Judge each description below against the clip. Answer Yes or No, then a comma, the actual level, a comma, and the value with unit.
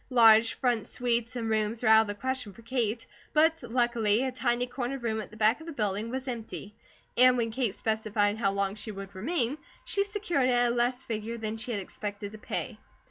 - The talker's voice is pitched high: Yes, high, 230 Hz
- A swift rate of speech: Yes, fast, 220 wpm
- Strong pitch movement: No, average, 2.7 semitones